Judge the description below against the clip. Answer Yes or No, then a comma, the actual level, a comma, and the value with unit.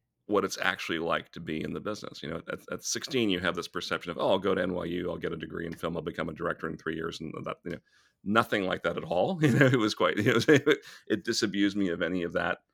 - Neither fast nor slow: No, fast, 285 wpm